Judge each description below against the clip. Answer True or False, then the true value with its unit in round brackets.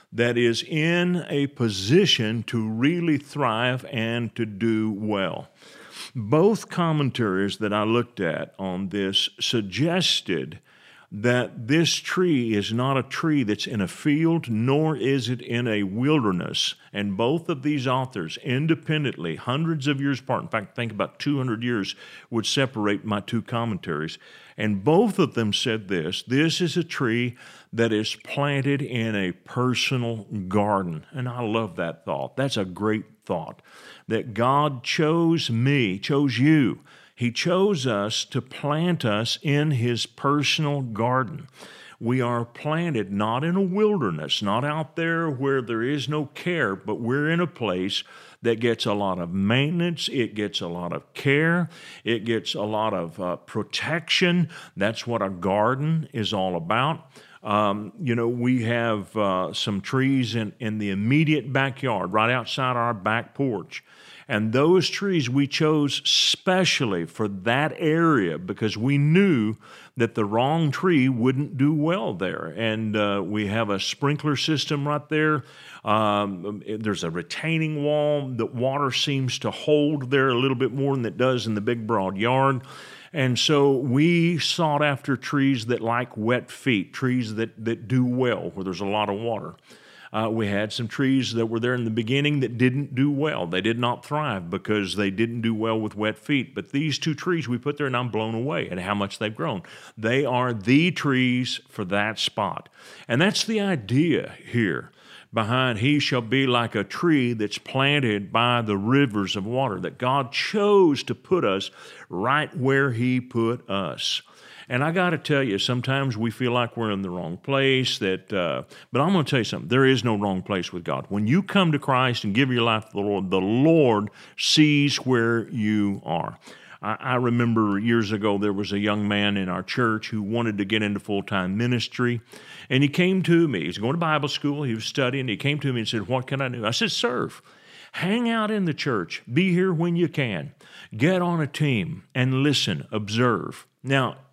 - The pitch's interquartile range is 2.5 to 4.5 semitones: False (5.1 semitones)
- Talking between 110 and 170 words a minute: False (180 wpm)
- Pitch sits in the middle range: False (125 Hz)